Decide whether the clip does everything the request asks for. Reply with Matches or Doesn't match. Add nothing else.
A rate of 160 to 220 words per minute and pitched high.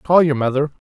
Doesn't match